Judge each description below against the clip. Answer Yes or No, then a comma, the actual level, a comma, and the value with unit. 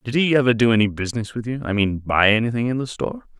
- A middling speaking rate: No, fast, 245 wpm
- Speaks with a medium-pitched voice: No, low, 120 Hz